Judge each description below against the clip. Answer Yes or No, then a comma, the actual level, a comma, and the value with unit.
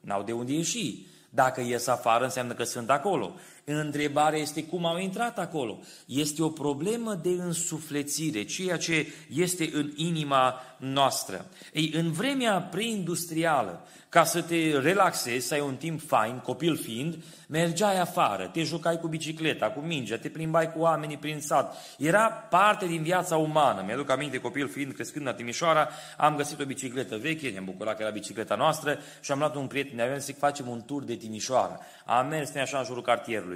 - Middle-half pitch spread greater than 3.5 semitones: Yes, average, 4.1 semitones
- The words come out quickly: Yes, fast, 180 wpm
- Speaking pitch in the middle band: Yes, medium, 150 Hz